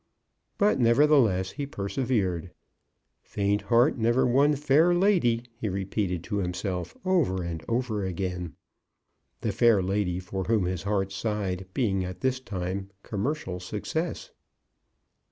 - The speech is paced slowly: Yes, slow, 125 wpm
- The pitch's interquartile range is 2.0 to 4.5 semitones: No, wide, 5.6 semitones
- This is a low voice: Yes, low, 105 Hz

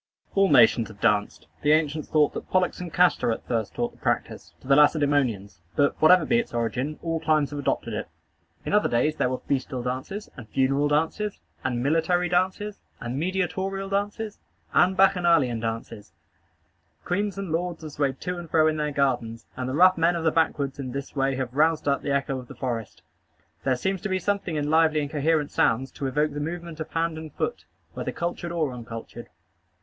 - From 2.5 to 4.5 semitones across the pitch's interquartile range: No, average, 4.9 semitones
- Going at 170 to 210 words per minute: Yes, average, 200 wpm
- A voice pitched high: No, medium, 150 Hz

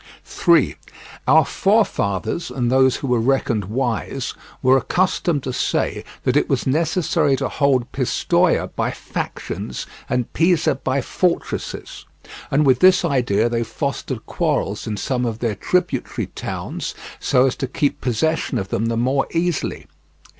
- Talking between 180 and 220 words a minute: No, average, 145 wpm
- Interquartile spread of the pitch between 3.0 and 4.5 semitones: No, average, 4.9 semitones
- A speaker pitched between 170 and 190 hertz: No, low, 130 Hz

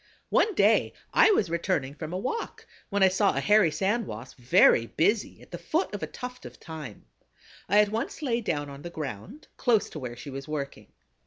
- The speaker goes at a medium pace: No, fast, 210 wpm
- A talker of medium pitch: Yes, medium, 180 Hz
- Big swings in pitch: Yes, wide, 7.7 semitones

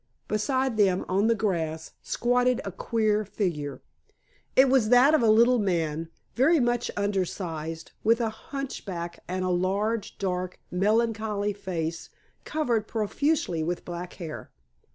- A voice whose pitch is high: Yes, high, 205 Hz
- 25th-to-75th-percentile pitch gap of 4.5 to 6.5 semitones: Yes, average, 4.8 semitones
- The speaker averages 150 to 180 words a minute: No, average, 140 wpm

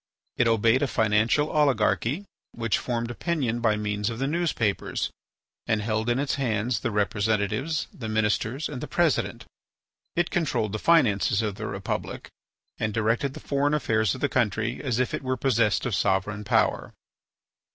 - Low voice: Yes, low, 115 Hz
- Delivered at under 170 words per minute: Yes, average, 160 wpm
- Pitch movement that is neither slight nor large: Yes, average, 4.1 semitones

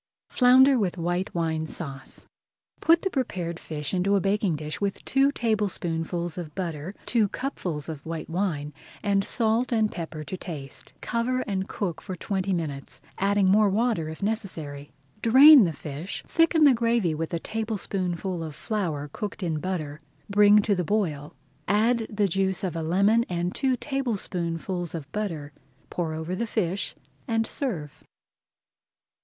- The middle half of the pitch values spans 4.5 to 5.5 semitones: Yes, average, 5.0 semitones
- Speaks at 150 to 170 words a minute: Yes, average, 160 wpm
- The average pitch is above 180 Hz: Yes, high, 190 Hz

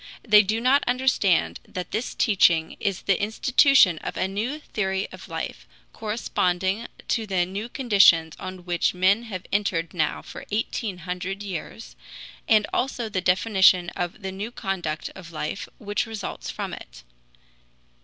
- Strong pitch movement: No, average, 3.5 semitones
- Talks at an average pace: Yes, average, 150 wpm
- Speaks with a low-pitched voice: No, high, 195 Hz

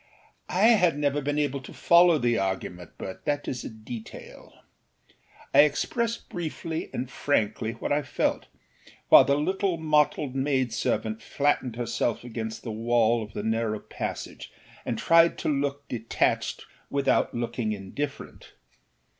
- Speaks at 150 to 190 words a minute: No, average, 140 wpm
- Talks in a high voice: No, low, 135 Hz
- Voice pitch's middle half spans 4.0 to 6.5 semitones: Yes, average, 4.7 semitones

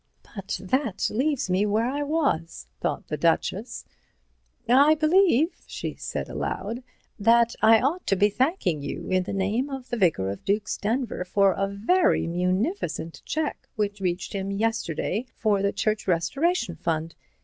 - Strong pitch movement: Yes, wide, 6.0 semitones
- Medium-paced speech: Yes, average, 155 wpm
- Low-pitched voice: No, high, 210 Hz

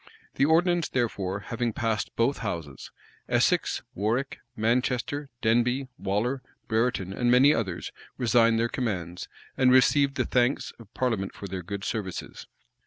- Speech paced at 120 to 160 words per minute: Yes, average, 140 wpm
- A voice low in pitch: Yes, low, 115 Hz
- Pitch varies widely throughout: No, average, 4.1 semitones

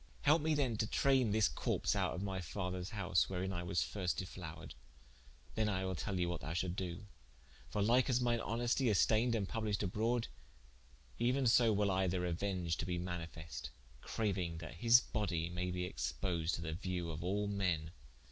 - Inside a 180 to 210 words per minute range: Yes, average, 190 wpm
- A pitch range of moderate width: Yes, average, 4.0 semitones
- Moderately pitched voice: No, very low, 95 Hz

